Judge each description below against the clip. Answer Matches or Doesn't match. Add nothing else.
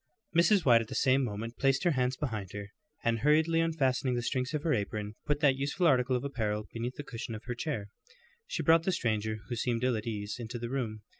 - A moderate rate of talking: Doesn't match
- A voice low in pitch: Matches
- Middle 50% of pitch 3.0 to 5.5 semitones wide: Matches